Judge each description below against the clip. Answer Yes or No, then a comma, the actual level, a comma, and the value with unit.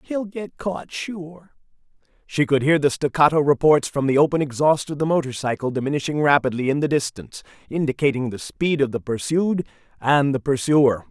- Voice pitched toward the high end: No, medium, 145 Hz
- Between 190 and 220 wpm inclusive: No, average, 170 wpm